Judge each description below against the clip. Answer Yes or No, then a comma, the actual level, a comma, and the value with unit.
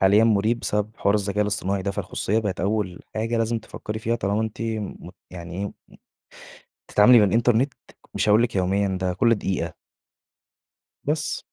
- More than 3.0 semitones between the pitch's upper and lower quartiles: No, narrow, 2.5 semitones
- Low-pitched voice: Yes, low, 105 Hz